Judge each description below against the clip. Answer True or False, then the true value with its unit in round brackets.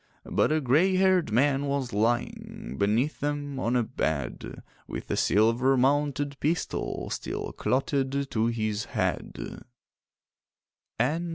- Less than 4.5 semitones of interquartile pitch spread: True (4.0 semitones)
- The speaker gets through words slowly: True (115 wpm)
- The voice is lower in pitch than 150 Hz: True (135 Hz)